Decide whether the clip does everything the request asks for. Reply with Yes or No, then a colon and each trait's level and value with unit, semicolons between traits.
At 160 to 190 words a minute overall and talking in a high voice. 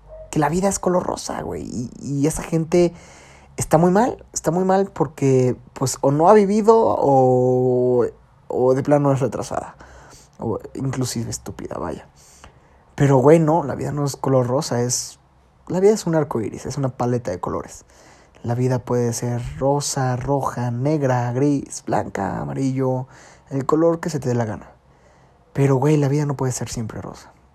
No: average, 175 wpm; low, 135 Hz